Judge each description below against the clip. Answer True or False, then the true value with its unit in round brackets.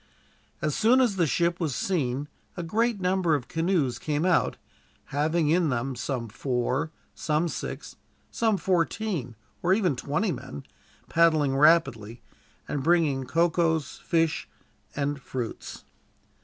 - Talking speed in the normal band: False (130 wpm)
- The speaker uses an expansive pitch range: False (4.3 semitones)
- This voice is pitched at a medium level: True (160 Hz)